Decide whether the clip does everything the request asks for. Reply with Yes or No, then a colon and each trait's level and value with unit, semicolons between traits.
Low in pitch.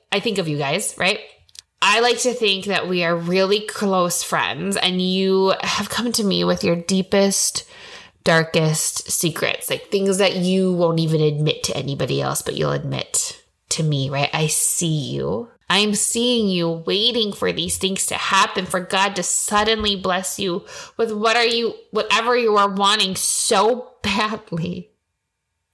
No: high, 195 Hz